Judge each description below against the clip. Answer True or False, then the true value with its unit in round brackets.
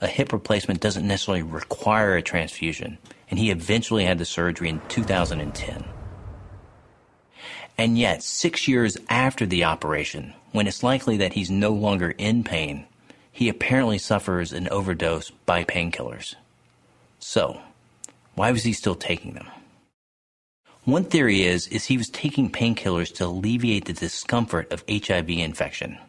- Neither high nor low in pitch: False (100 Hz)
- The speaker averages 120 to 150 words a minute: True (140 wpm)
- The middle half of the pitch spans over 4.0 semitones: True (4.8 semitones)